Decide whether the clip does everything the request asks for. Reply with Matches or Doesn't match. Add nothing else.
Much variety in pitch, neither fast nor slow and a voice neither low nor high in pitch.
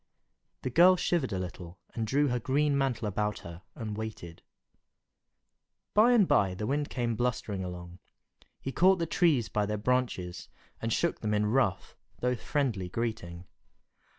Doesn't match